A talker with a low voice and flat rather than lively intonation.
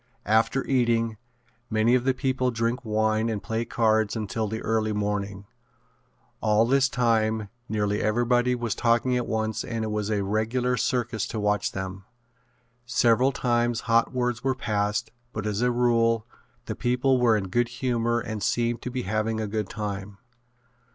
Yes: low, 115 Hz; narrow, 2.1 semitones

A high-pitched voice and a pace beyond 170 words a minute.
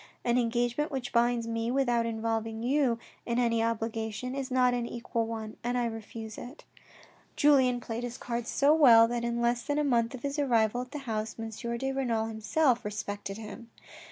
Yes: high, 235 Hz; average, 185 wpm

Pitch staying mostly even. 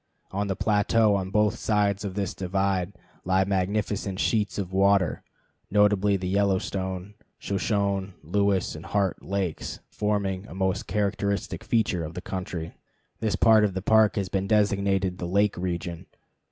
Yes: narrow, 1.6 semitones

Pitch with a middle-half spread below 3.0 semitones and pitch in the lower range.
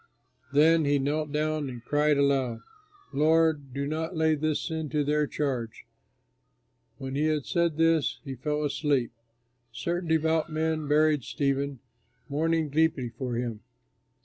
No: narrow, 2.4 semitones; medium, 150 Hz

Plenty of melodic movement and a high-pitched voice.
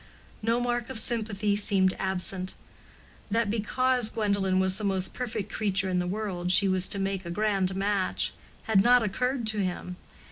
No: average, 2.7 semitones; high, 200 Hz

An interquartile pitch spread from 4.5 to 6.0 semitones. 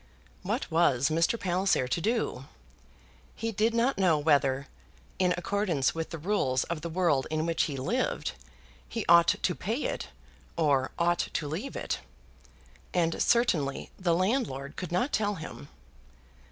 Yes: average, 5.1 semitones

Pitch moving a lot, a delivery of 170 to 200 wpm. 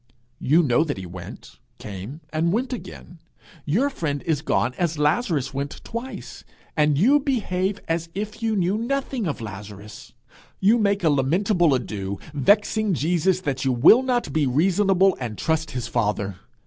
No: wide, 7.6 semitones; average, 160 wpm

